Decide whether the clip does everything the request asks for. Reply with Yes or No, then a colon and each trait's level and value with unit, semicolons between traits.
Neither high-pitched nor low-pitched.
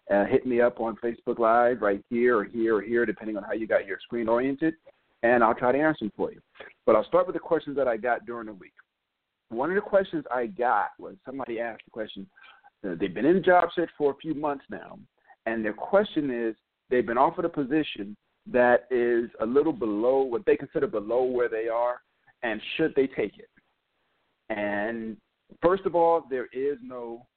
No: low, 125 Hz